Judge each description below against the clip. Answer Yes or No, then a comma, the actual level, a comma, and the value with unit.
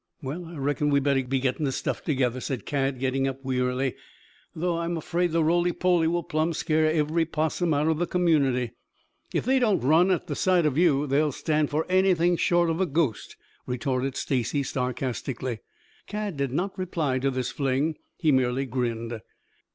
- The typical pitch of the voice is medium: Yes, medium, 145 Hz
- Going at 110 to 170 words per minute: No, average, 180 wpm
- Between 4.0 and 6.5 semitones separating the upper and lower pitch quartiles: Yes, average, 4.3 semitones